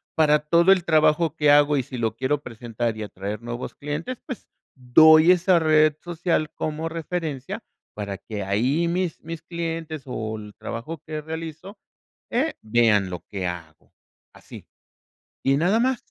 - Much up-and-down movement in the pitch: Yes, wide, 6.1 semitones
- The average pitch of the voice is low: No, medium, 150 Hz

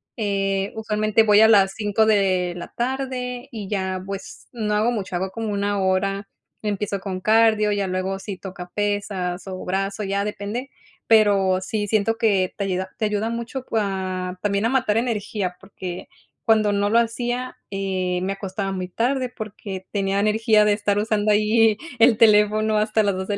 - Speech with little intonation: Yes, narrow, 2.2 semitones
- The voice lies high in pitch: Yes, high, 205 Hz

